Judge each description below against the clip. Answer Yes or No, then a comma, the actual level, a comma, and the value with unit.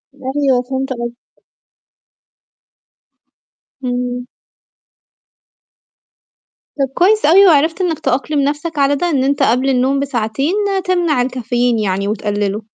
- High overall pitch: Yes, very high, 265 Hz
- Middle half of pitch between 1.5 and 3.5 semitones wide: Yes, average, 3.2 semitones